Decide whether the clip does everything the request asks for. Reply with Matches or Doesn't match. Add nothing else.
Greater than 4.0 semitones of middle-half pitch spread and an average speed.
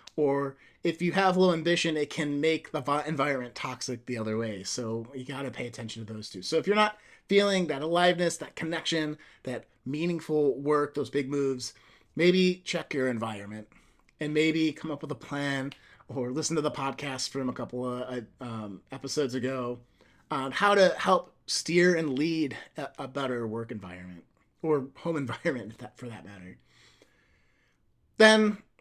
Matches